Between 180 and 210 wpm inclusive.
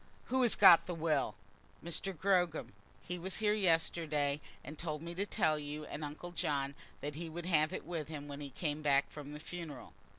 Yes: average, 200 wpm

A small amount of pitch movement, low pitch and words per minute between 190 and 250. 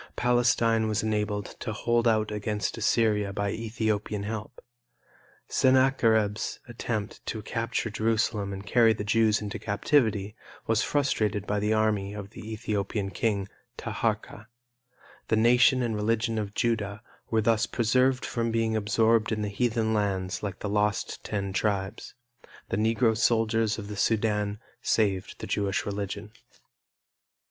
No: narrow, 1.7 semitones; low, 110 Hz; slow, 135 wpm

